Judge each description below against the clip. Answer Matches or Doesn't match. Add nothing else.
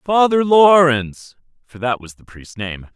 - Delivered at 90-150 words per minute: Matches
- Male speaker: Matches